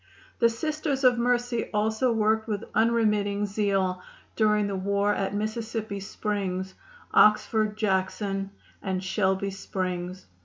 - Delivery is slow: Yes, slow, 115 wpm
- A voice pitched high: Yes, high, 210 Hz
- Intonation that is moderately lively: No, narrow, 2.2 semitones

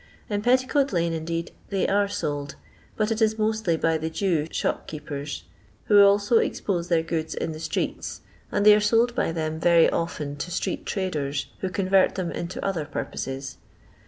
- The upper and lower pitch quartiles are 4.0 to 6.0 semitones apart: Yes, average, 4.4 semitones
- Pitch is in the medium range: Yes, medium, 175 Hz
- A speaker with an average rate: Yes, average, 170 wpm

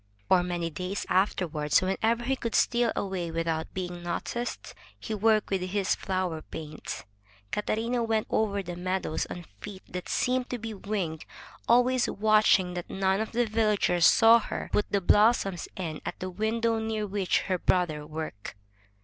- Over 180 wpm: No, average, 165 wpm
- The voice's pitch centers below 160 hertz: No, high, 195 Hz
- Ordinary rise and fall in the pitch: Yes, average, 3.9 semitones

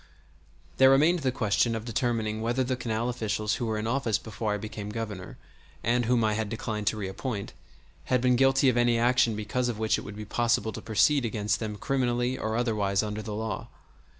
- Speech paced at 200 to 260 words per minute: Yes, fast, 205 wpm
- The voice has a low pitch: Yes, low, 115 Hz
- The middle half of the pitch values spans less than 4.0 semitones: Yes, narrow, 2.4 semitones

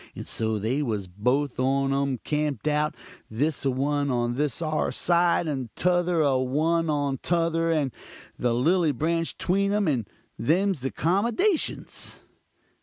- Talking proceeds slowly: No, average, 150 wpm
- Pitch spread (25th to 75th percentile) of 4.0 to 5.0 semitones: Yes, average, 4.3 semitones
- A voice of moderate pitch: Yes, medium, 150 Hz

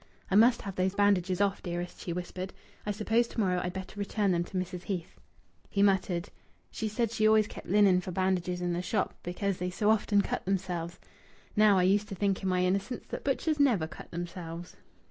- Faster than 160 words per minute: Yes, fast, 205 wpm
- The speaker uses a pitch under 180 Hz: No, high, 190 Hz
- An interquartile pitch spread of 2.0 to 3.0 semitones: Yes, narrow, 2.5 semitones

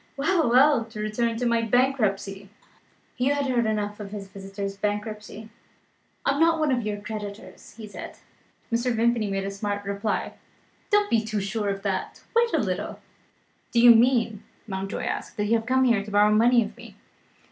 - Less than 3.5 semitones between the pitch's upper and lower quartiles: Yes, average, 3.0 semitones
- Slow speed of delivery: No, average, 190 wpm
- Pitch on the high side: Yes, high, 220 Hz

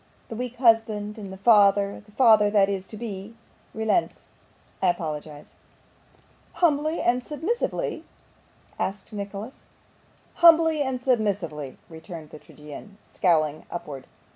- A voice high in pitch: Yes, high, 205 Hz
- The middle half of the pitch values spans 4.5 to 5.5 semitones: Yes, average, 5.1 semitones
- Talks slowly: Yes, slow, 120 wpm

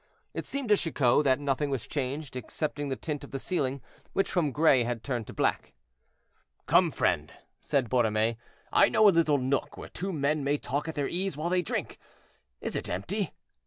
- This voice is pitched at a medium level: Yes, medium, 145 Hz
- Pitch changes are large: No, average, 3.9 semitones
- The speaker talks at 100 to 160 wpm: No, average, 195 wpm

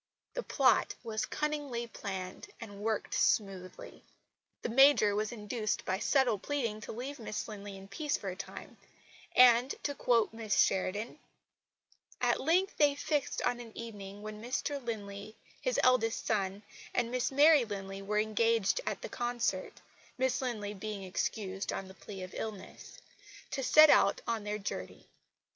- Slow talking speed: No, average, 155 wpm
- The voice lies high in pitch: Yes, high, 220 Hz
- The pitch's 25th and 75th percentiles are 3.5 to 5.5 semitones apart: Yes, average, 3.9 semitones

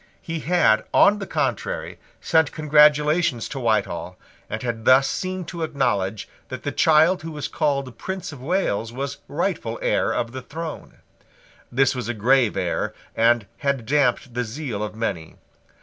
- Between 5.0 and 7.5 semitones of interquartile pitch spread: Yes, average, 5.3 semitones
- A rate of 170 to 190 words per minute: No, average, 160 wpm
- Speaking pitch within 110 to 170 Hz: Yes, low, 135 Hz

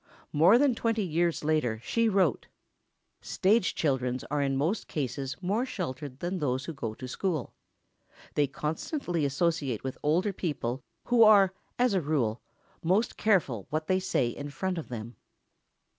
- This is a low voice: No, medium, 155 Hz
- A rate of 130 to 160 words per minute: Yes, average, 155 wpm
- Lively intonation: Yes, wide, 6.1 semitones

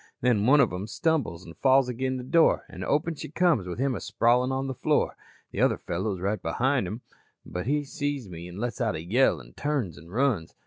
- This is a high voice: No, low, 120 Hz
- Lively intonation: Yes, wide, 6.8 semitones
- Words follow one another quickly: Yes, fast, 230 wpm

